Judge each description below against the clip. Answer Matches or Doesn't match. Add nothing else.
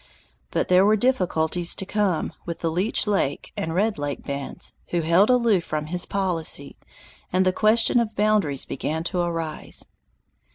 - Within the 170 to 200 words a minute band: Doesn't match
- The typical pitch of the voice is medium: Matches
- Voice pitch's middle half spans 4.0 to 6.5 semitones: Matches